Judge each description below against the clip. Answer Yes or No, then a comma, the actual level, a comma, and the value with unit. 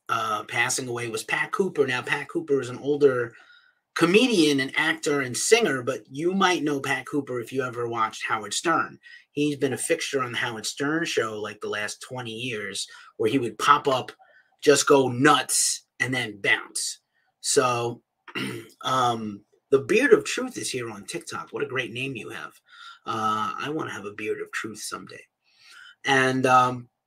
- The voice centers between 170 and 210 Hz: Yes, medium, 185 Hz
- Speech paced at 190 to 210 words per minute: No, average, 180 wpm